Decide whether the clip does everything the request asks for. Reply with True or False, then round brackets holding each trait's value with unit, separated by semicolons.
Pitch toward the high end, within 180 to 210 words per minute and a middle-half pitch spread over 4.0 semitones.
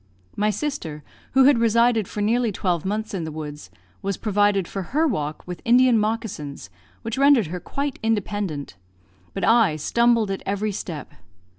False (210 Hz; 160 wpm; 4.9 semitones)